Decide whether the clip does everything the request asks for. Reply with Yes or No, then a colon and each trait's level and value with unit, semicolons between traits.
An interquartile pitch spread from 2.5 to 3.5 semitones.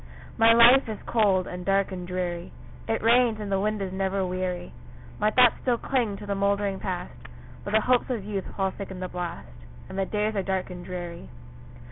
Yes: average, 2.8 semitones